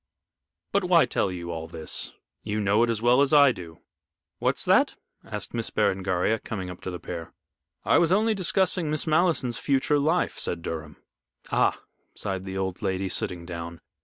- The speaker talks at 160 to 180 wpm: Yes, average, 175 wpm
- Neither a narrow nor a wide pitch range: No, wide, 8.9 semitones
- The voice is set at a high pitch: No, low, 100 Hz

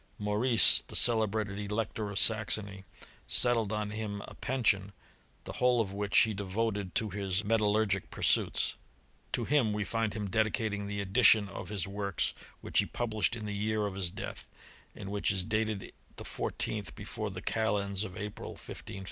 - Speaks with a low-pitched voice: Yes, low, 105 Hz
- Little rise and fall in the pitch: Yes, narrow, 1.7 semitones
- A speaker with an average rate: Yes, average, 165 wpm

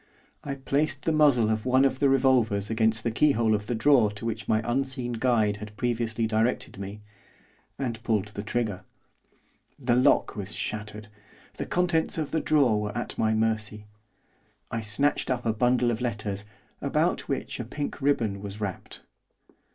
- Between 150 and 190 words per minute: Yes, average, 165 wpm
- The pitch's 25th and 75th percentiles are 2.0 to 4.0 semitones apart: Yes, average, 3.6 semitones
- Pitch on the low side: Yes, low, 115 Hz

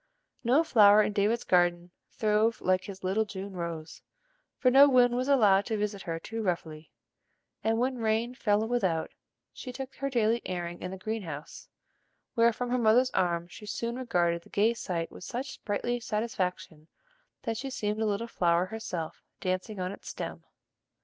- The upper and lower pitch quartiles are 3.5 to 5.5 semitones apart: Yes, average, 4.5 semitones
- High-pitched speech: Yes, high, 210 Hz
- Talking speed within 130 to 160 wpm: No, average, 175 wpm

